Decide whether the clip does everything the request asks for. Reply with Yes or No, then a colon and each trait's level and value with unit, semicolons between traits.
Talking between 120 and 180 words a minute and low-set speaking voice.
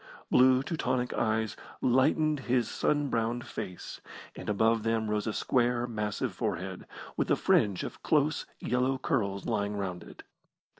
Yes: average, 145 wpm; low, 115 Hz